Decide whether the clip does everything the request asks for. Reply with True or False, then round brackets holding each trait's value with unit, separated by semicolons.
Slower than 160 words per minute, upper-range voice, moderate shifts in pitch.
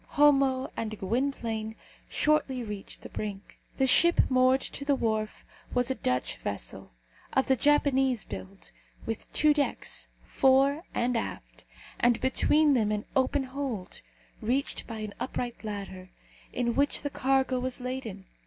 True (145 wpm; 255 Hz; 3.8 semitones)